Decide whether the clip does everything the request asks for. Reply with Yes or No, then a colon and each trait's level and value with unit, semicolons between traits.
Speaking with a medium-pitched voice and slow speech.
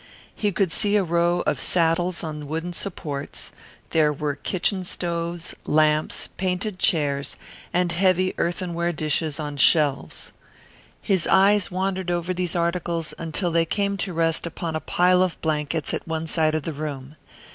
No: medium, 170 Hz; average, 155 wpm